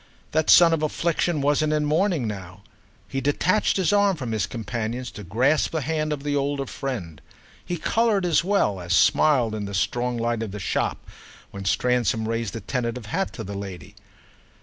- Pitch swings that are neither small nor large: No, wide, 6.1 semitones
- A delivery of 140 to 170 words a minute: No, average, 185 wpm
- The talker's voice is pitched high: No, low, 130 Hz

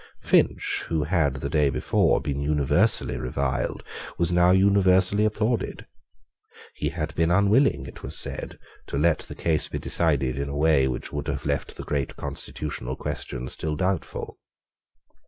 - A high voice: No, very low, 75 Hz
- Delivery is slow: No, average, 155 wpm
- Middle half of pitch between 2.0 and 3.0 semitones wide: No, average, 4.3 semitones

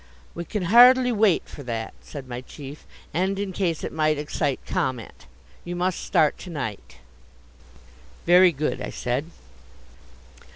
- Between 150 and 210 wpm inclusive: No, average, 140 wpm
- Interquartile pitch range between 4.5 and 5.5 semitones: Yes, average, 5.1 semitones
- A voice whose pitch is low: No, medium, 160 Hz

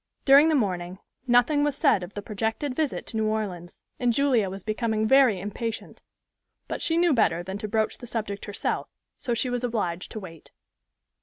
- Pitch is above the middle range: Yes, high, 220 Hz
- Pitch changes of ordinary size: Yes, average, 4.1 semitones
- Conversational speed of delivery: Yes, average, 185 wpm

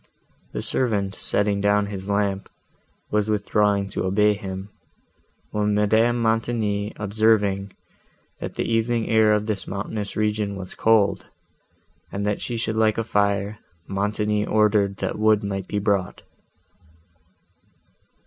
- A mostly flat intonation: Yes, narrow, 1.3 semitones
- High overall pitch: No, low, 105 Hz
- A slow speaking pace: Yes, slow, 130 wpm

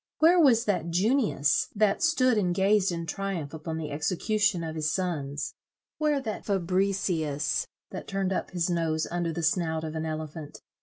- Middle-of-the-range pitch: Yes, medium, 175 Hz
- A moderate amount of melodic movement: Yes, average, 4.3 semitones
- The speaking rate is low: No, average, 165 wpm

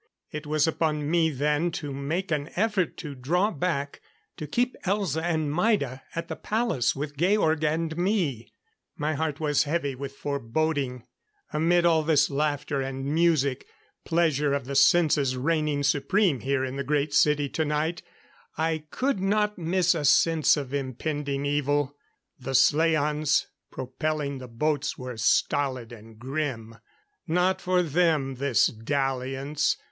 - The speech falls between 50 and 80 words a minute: No, average, 140 wpm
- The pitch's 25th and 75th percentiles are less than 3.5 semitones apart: Yes, average, 3.0 semitones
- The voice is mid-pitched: Yes, medium, 150 Hz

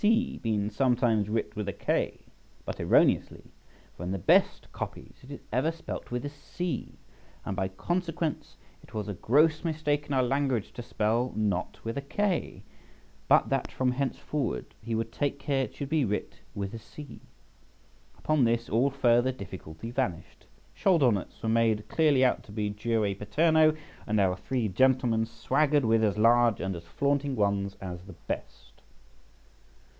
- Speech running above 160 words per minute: Yes, average, 170 wpm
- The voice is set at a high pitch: No, low, 120 Hz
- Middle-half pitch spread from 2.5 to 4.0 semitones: No, average, 5.3 semitones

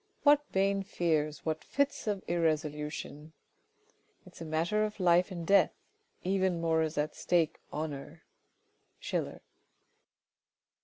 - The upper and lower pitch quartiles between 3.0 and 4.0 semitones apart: Yes, average, 3.6 semitones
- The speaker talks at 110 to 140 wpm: Yes, slow, 135 wpm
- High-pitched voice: No, medium, 170 Hz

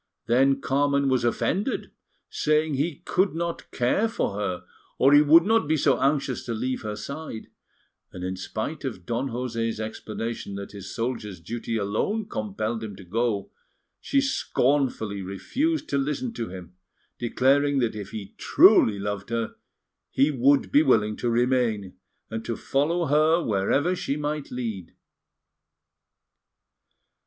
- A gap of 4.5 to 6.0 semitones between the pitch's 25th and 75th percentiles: Yes, average, 5.3 semitones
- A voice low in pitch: Yes, low, 125 Hz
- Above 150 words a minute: No, average, 145 wpm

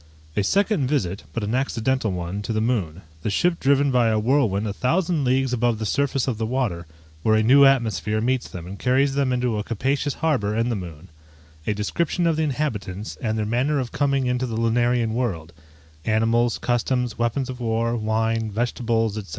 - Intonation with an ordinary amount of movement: Yes, average, 3.5 semitones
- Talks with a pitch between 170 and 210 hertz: No, low, 120 Hz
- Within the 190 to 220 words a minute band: Yes, average, 195 wpm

